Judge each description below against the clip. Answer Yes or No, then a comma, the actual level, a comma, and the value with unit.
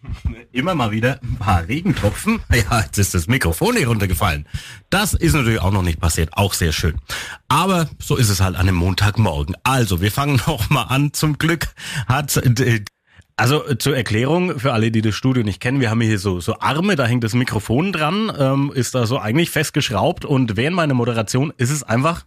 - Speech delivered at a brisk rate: Yes, fast, 195 wpm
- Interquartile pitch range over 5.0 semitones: Yes, wide, 5.5 semitones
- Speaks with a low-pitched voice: Yes, low, 125 Hz